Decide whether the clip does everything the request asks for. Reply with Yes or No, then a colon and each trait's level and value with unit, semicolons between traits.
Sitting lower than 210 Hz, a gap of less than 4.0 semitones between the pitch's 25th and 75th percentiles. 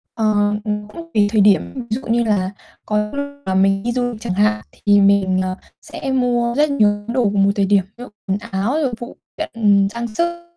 No: high, 215 Hz; average, 3.3 semitones